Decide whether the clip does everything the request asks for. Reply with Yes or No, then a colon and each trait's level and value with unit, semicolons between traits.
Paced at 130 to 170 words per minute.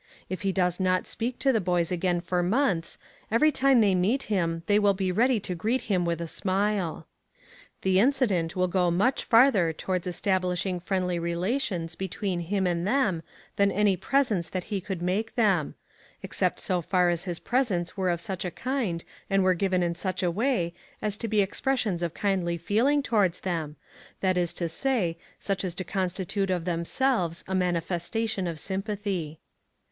No: average, 180 wpm